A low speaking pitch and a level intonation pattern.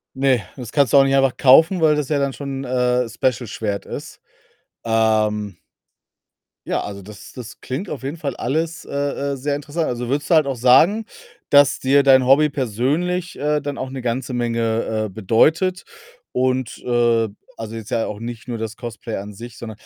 No: low, 130 Hz; average, 3.8 semitones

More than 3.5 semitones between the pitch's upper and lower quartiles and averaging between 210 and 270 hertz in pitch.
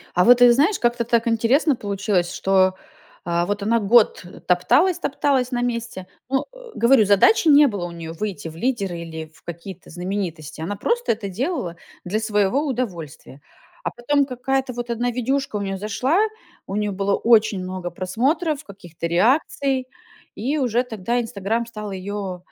Yes: average, 5.1 semitones; high, 215 Hz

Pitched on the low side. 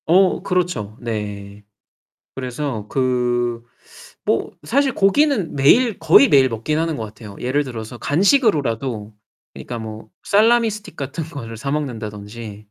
Yes: low, 130 Hz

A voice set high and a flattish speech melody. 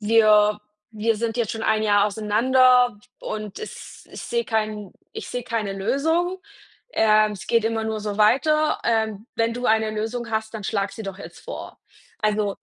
Yes: high, 220 Hz; narrow, 1.9 semitones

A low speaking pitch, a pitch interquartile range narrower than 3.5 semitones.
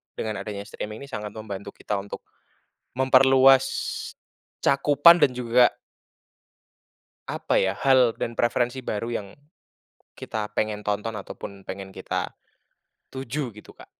No: low, 115 Hz; average, 4.1 semitones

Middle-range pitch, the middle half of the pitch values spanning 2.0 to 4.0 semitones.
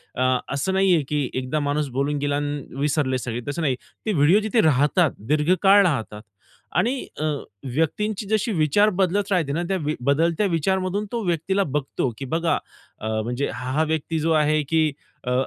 No: medium, 155 Hz; average, 4.8 semitones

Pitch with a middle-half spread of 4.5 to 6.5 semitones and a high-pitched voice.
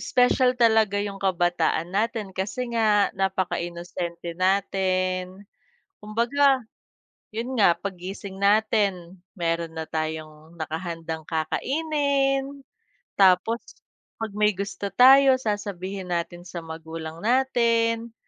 Yes: average, 4.9 semitones; high, 195 Hz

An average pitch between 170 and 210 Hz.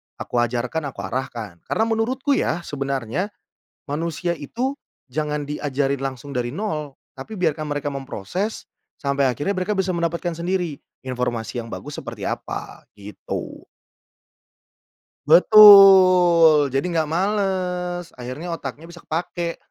No: medium, 155 Hz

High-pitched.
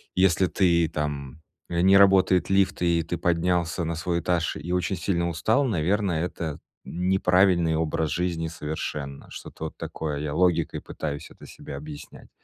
No: very low, 85 Hz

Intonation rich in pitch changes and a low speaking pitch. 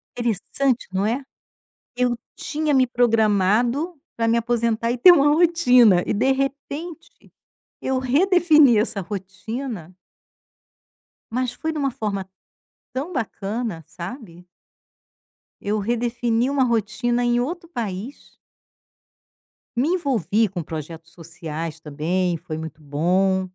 No: wide, 5.9 semitones; high, 235 Hz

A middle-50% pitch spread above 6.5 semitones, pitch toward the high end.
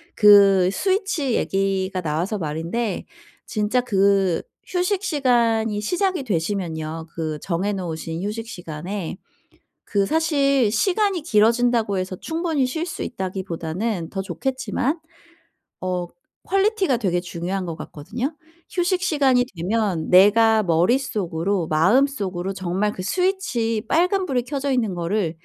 Yes: wide, 6.9 semitones; high, 210 Hz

